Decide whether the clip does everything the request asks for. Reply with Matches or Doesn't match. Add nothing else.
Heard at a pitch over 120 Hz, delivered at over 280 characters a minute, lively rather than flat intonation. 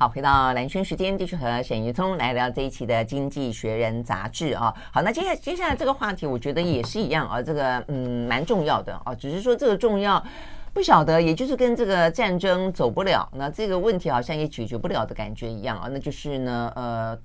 Matches